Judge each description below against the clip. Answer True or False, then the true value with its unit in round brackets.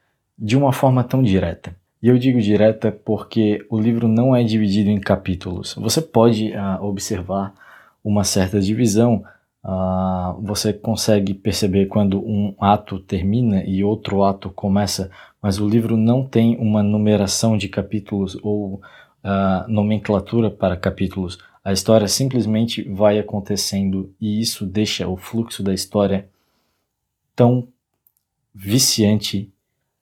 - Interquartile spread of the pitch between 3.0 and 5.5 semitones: False (2.5 semitones)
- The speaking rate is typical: True (130 wpm)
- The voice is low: True (105 Hz)